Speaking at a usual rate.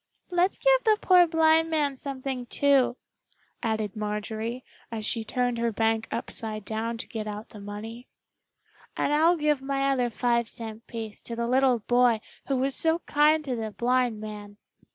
Yes: average, 170 wpm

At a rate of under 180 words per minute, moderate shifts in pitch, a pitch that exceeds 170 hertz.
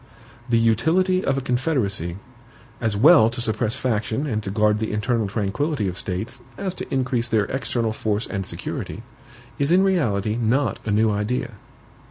No: average, 165 wpm; average, 4.1 semitones; low, 115 Hz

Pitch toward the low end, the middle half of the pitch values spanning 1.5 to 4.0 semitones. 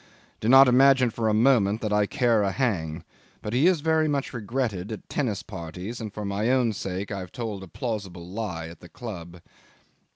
No: low, 110 Hz; average, 4.6 semitones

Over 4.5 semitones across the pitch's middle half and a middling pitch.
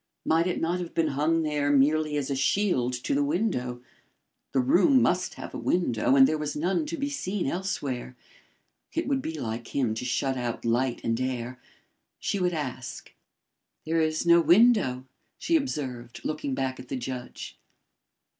Yes: wide, 5.5 semitones; medium, 145 Hz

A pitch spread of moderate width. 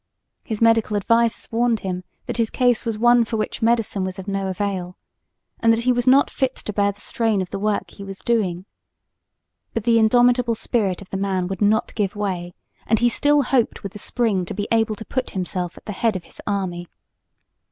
Yes: average, 3.3 semitones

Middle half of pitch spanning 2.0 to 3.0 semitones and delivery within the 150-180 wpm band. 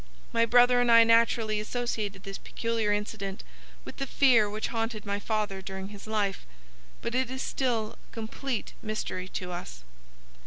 Yes: narrow, 2.6 semitones; average, 160 wpm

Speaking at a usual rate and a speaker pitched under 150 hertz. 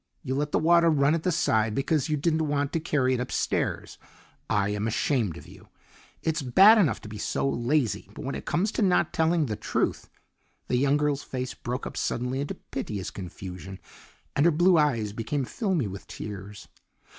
Yes: average, 195 wpm; medium, 140 Hz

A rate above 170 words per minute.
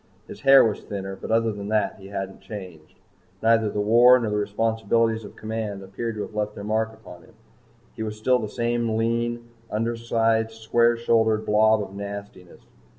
Yes: average, 180 wpm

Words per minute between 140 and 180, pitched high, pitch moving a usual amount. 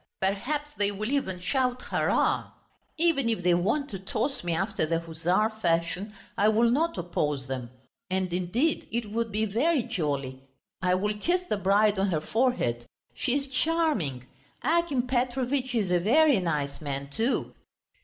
No: average, 160 wpm; high, 210 Hz; wide, 6.7 semitones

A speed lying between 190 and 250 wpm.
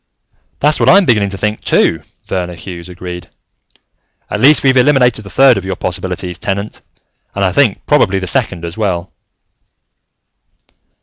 No: average, 150 wpm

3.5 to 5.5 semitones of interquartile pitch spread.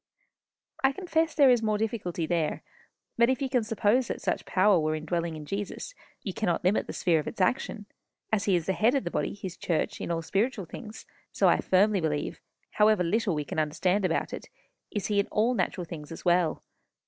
Yes: average, 4.7 semitones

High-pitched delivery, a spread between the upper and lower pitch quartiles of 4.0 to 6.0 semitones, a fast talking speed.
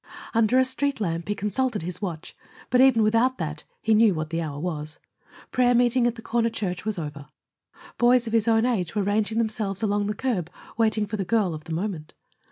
Yes: high, 215 Hz; average, 4.8 semitones; fast, 210 wpm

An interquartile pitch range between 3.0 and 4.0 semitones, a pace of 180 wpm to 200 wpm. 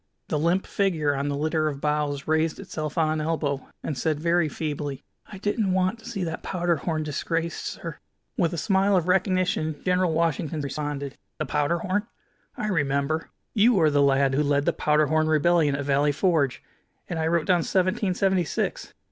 Yes: average, 3.7 semitones; average, 190 wpm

